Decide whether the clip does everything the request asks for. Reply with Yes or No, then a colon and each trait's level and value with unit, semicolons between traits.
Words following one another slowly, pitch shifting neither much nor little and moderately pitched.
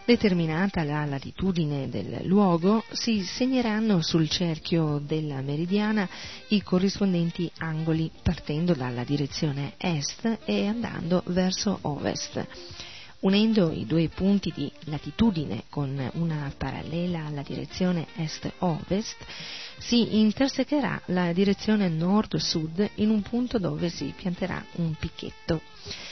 Yes: slow, 110 wpm; average, 5.0 semitones; medium, 175 Hz